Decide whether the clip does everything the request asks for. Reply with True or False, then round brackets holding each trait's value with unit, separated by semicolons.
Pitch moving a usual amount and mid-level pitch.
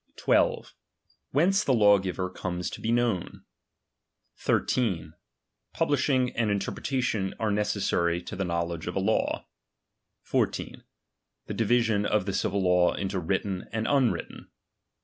False (4.5 semitones; 100 Hz)